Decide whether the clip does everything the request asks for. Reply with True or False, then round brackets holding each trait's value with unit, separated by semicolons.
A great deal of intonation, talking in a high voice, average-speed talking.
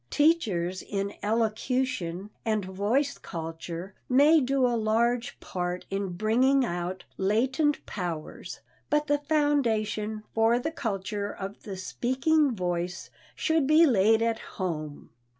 False (5.9 semitones; 220 Hz; 120 wpm)